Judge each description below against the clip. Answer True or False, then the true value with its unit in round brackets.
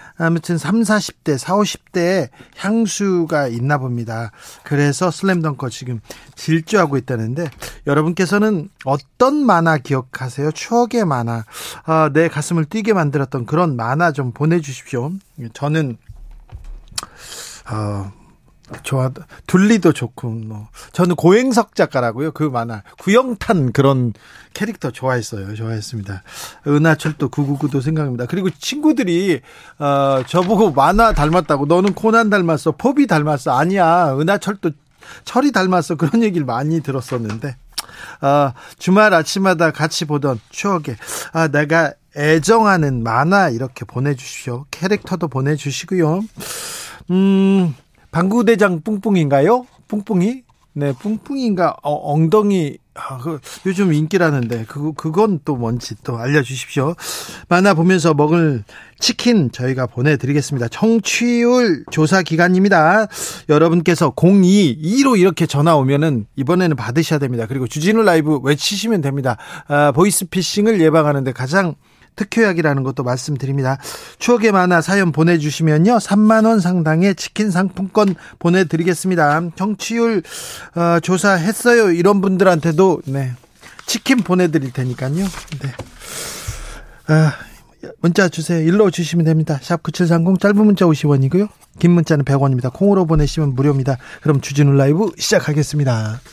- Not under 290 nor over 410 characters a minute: True (300 characters per minute)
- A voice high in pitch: False (160 Hz)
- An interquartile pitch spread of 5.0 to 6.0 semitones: True (5.6 semitones)